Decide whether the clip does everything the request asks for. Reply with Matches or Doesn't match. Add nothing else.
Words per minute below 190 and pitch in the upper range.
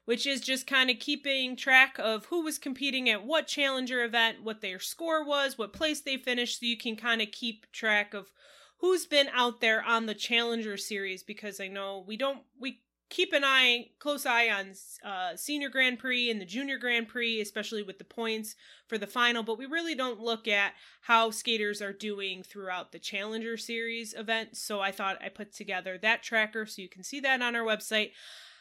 Doesn't match